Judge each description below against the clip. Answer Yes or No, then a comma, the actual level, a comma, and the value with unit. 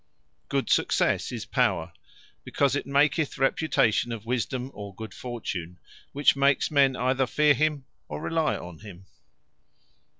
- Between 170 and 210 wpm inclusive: No, slow, 135 wpm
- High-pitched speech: No, low, 130 Hz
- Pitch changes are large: No, average, 4.5 semitones